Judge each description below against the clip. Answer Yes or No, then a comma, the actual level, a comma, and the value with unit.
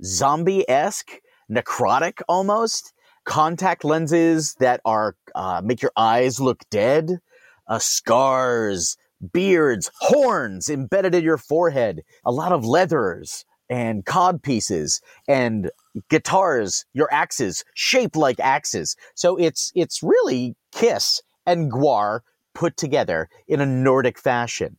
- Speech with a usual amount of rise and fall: No, wide, 6.2 semitones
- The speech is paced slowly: Yes, slow, 120 wpm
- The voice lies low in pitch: No, medium, 155 Hz